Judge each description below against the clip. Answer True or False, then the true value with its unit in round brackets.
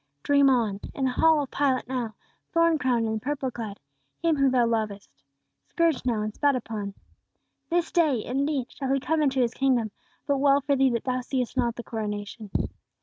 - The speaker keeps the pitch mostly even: False (3.6 semitones)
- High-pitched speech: True (255 Hz)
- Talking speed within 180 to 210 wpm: True (190 wpm)